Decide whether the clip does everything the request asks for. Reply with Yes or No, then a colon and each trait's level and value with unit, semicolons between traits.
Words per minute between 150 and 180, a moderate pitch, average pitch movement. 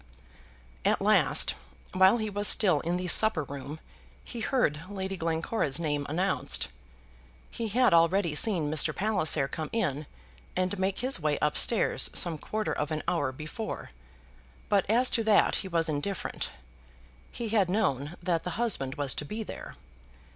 No: average, 155 wpm; medium, 180 Hz; wide, 5.7 semitones